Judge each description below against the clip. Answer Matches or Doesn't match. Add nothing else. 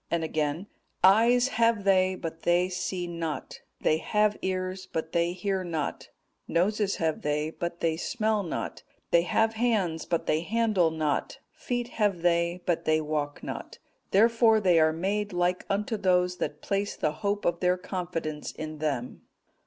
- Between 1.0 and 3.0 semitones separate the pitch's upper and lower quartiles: Doesn't match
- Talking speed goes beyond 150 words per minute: Matches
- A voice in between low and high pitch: Matches